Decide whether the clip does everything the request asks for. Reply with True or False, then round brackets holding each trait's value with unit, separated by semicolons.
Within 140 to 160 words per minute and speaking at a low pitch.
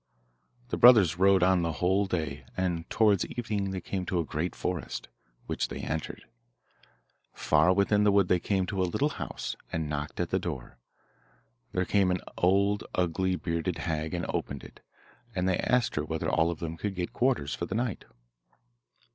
False (180 wpm; 90 Hz)